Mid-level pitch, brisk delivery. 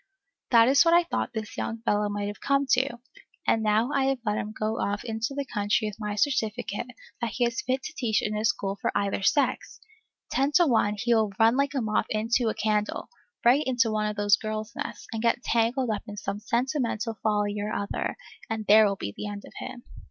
No: high, 220 Hz; fast, 225 wpm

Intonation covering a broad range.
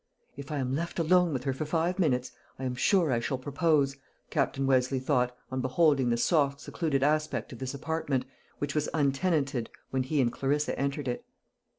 No: average, 3.0 semitones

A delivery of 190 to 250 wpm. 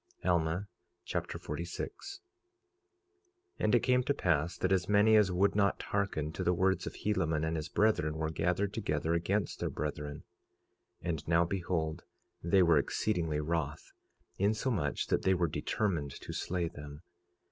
No: average, 160 wpm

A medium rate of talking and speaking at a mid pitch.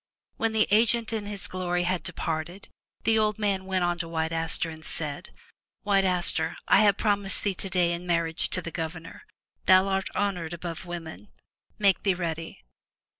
Yes: average, 170 wpm; medium, 180 Hz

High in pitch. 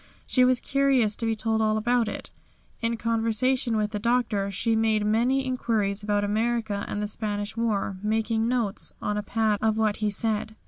Yes: high, 220 Hz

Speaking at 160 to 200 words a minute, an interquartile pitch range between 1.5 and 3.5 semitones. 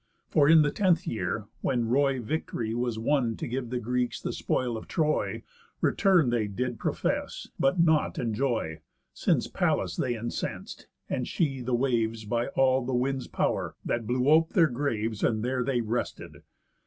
Yes: average, 165 wpm; average, 3.1 semitones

